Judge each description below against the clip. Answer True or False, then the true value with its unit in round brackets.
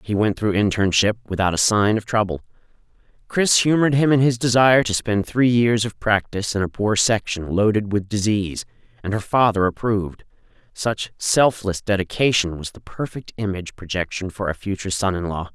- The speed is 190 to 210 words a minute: False (180 wpm)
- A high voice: False (105 Hz)